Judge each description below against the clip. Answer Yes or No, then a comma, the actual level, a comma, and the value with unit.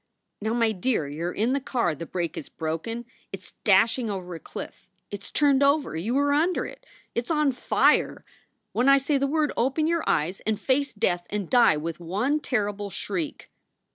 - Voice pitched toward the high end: Yes, high, 225 Hz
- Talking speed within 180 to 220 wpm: Yes, average, 200 wpm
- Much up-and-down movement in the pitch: Yes, wide, 7.3 semitones